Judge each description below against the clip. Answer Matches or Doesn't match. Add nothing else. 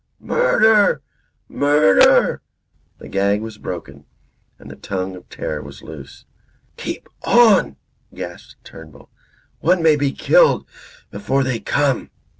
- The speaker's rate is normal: Doesn't match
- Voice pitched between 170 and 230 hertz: Doesn't match